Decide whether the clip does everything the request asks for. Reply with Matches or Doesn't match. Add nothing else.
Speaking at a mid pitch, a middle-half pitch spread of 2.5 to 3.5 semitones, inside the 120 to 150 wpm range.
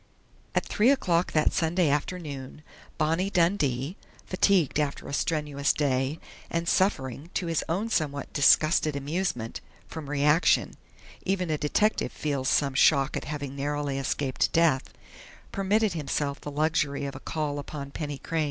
Matches